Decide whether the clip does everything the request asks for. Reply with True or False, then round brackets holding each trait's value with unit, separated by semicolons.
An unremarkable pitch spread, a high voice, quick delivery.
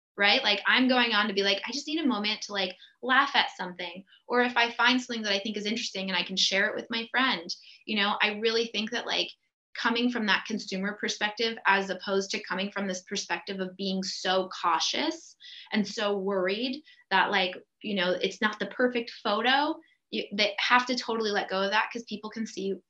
True (3.3 semitones; 210 Hz; 220 wpm)